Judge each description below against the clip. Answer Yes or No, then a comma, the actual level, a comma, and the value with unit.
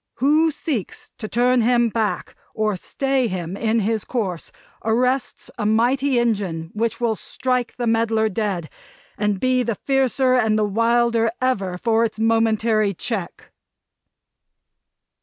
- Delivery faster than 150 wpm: No, slow, 135 wpm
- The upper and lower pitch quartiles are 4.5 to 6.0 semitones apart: No, average, 2.7 semitones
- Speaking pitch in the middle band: No, high, 225 Hz